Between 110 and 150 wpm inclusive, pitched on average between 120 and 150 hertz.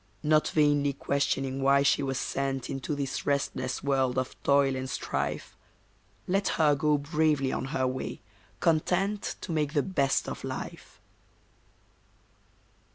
Yes: slow, 135 wpm; medium, 140 Hz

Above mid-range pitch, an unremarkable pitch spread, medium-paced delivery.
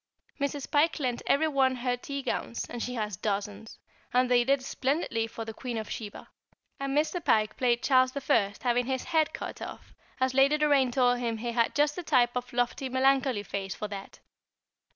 Yes: very high, 250 Hz; average, 3.1 semitones; average, 190 wpm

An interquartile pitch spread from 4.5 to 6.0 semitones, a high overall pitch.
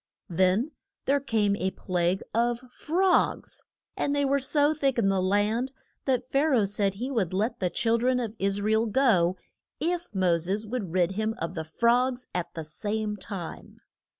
Yes: average, 5.2 semitones; high, 215 Hz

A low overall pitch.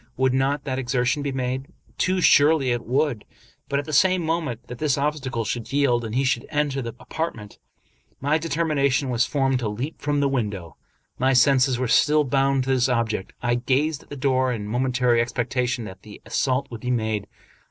Yes: low, 130 Hz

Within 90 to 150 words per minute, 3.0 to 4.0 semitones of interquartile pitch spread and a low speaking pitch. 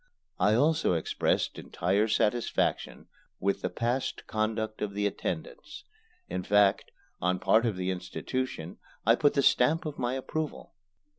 No: average, 140 wpm; average, 4.7 semitones; low, 110 Hz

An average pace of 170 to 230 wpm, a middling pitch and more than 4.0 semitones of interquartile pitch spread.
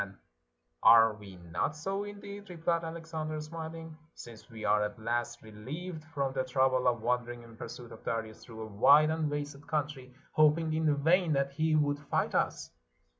Yes: average, 175 wpm; medium, 145 Hz; average, 5.1 semitones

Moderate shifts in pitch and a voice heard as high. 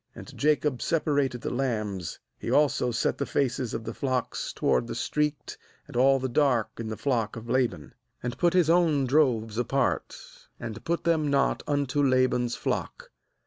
No: average, 3.6 semitones; low, 130 Hz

